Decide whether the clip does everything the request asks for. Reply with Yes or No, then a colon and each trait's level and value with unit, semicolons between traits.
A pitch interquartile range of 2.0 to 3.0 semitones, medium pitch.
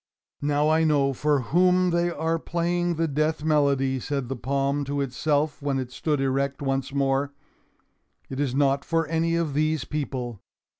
Yes: average, 2.7 semitones; medium, 145 Hz